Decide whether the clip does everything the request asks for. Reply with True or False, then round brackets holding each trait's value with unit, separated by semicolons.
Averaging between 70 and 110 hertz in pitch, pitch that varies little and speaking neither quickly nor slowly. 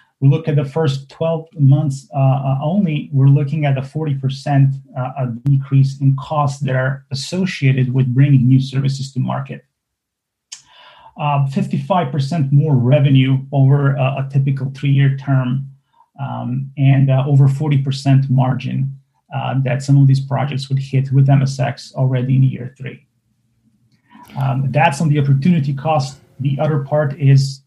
False (135 Hz; 1.3 semitones; 145 wpm)